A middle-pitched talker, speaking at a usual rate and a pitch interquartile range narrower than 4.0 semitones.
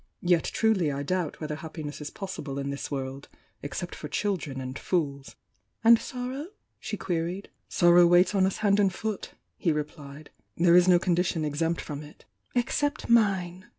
No: medium, 175 Hz; average, 170 wpm; average, 4.6 semitones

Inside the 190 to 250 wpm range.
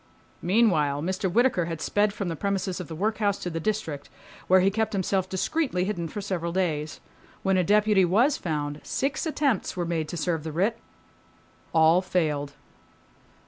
No: average, 170 wpm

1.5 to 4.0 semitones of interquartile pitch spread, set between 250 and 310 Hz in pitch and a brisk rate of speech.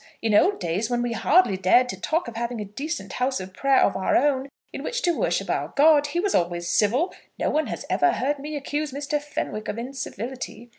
No: wide, 5.6 semitones; very high, 260 Hz; fast, 225 wpm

